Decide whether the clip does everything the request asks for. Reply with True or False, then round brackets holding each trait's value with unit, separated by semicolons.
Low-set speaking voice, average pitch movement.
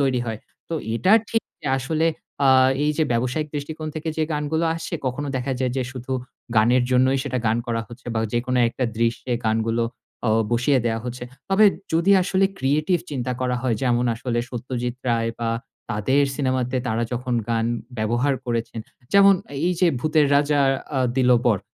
True (130 Hz; 3.8 semitones)